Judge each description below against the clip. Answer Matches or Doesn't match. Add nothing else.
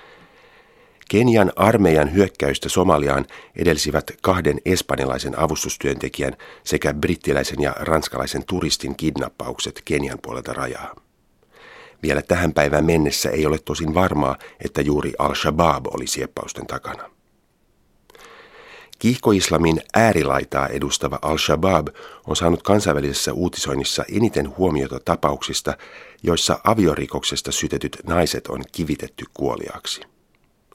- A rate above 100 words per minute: Doesn't match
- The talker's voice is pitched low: Matches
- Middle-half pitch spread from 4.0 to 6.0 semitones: Matches